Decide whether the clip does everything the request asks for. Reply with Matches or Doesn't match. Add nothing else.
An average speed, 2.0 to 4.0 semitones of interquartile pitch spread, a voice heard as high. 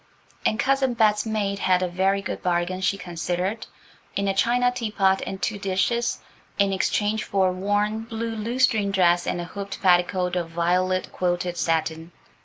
Matches